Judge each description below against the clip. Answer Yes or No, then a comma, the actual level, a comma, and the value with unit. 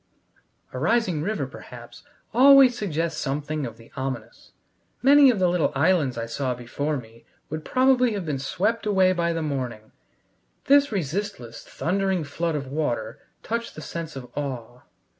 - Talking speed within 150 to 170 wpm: Yes, average, 155 wpm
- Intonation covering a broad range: Yes, wide, 7.3 semitones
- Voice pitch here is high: No, medium, 155 Hz